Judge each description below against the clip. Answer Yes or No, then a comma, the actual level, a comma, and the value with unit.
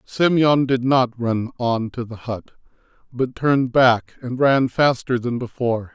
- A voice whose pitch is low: Yes, low, 125 Hz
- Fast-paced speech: No, average, 160 wpm